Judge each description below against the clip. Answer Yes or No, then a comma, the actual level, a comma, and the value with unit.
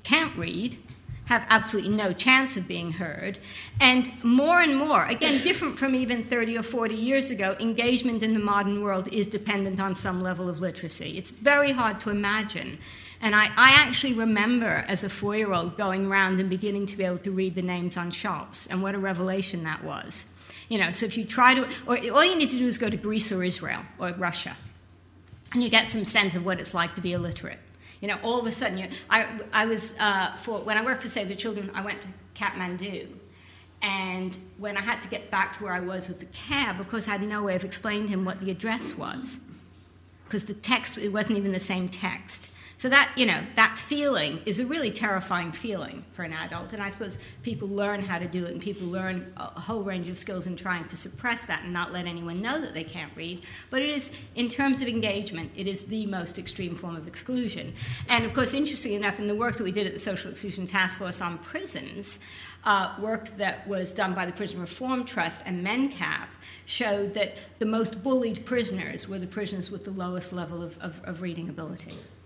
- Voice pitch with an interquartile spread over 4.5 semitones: No, average, 3.8 semitones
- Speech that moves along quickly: Yes, fast, 225 wpm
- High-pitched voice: Yes, high, 200 Hz